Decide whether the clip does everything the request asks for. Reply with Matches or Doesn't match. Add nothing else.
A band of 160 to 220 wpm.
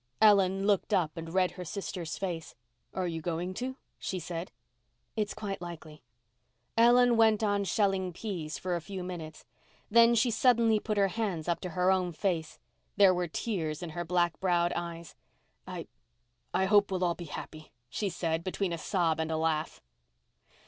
Matches